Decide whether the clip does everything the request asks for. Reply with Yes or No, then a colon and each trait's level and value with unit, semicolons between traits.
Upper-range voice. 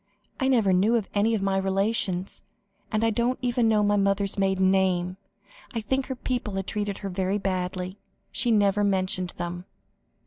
Yes: high, 200 Hz